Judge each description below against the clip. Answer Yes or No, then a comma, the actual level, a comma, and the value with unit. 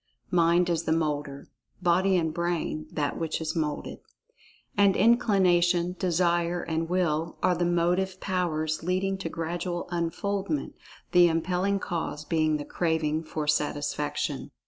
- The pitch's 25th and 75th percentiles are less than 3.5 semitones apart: Yes, narrow, 2.4 semitones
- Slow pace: Yes, slow, 125 wpm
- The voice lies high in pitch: No, medium, 170 Hz